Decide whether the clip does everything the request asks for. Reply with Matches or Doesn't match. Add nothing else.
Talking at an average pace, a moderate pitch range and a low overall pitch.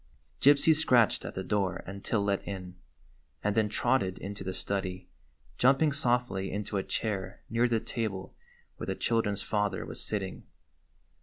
Matches